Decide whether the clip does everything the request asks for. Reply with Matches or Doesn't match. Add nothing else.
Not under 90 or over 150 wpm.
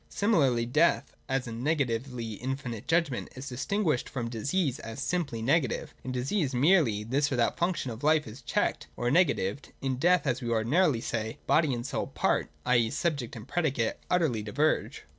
Doesn't match